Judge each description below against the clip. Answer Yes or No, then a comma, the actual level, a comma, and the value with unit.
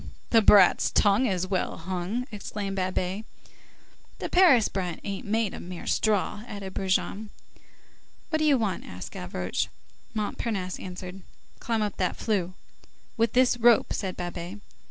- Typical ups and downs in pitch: Yes, average, 3.2 semitones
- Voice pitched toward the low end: No, high, 200 Hz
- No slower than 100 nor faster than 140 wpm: Yes, slow, 135 wpm